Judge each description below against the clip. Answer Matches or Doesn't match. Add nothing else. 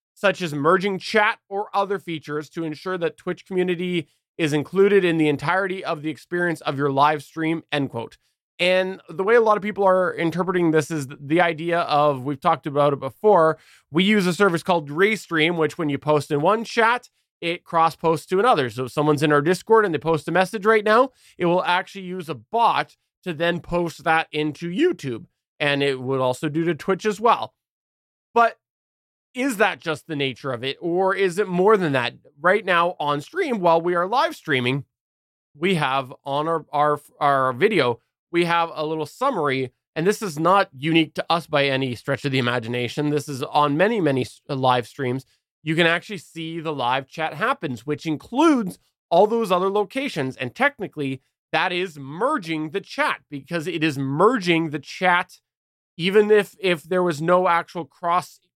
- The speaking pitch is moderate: Matches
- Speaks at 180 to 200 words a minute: Matches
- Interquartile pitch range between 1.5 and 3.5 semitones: Doesn't match